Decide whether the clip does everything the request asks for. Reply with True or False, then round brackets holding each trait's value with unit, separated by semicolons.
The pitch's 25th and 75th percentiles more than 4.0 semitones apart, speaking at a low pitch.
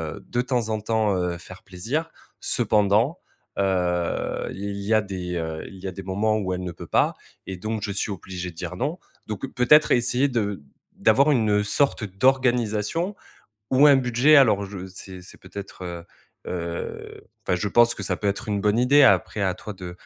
True (4.5 semitones; 105 Hz)